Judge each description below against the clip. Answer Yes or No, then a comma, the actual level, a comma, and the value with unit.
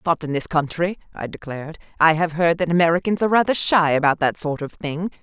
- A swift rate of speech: Yes, fast, 220 wpm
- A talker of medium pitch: Yes, medium, 165 Hz